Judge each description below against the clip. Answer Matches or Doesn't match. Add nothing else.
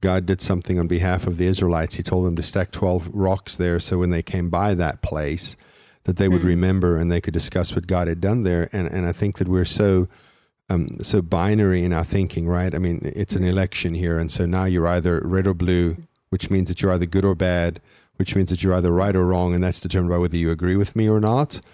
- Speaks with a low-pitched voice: Matches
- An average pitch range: Doesn't match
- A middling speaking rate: Doesn't match